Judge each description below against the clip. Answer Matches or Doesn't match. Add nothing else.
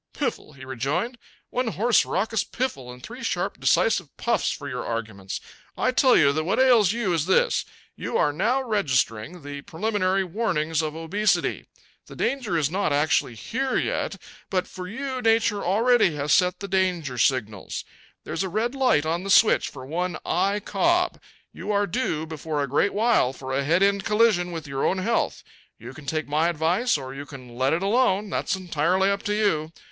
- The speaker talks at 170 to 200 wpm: Matches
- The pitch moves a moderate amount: Doesn't match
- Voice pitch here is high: Doesn't match